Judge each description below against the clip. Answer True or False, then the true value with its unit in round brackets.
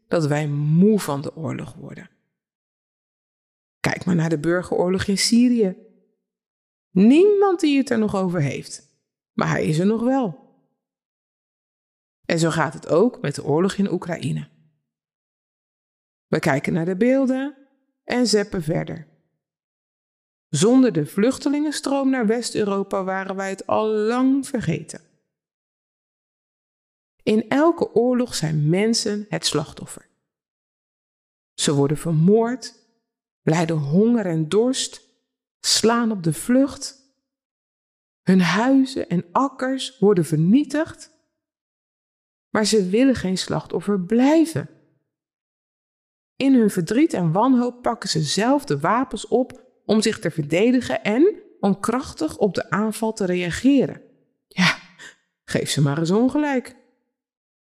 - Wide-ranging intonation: True (6.9 semitones)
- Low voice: False (215 Hz)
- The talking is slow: True (120 wpm)